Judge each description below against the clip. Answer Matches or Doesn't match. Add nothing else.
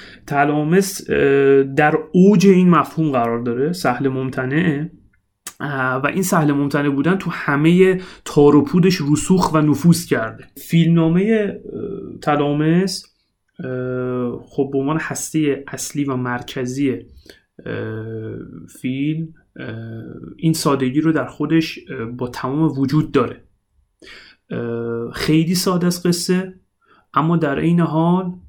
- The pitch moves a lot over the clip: Doesn't match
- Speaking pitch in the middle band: Matches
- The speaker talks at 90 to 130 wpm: Matches